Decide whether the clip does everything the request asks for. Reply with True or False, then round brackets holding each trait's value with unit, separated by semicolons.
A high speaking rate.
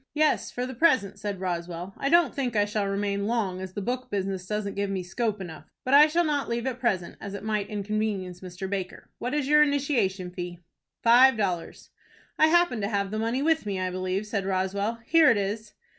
True (215 wpm)